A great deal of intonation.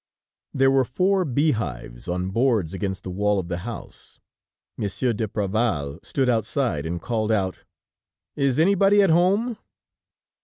Yes: wide, 6.7 semitones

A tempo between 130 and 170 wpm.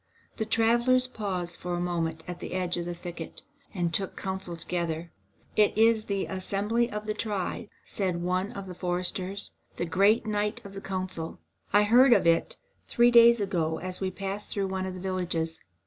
No: average, 185 wpm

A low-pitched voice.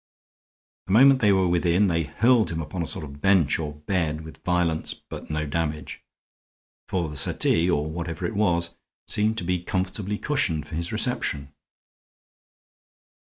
Yes: very low, 85 Hz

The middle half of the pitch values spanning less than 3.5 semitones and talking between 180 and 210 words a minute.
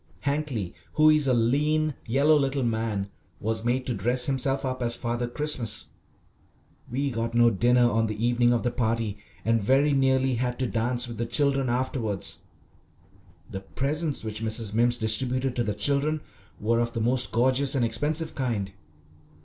No: average, 3.0 semitones; average, 165 wpm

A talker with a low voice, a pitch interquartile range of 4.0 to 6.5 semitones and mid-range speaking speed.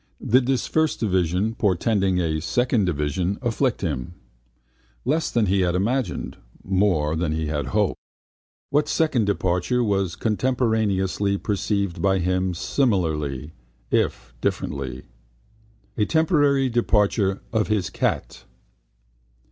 No: low, 100 Hz; average, 5.2 semitones; slow, 115 wpm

